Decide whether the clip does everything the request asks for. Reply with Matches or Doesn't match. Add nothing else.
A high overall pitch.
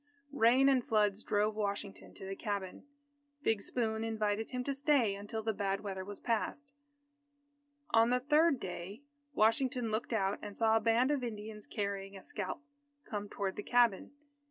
Matches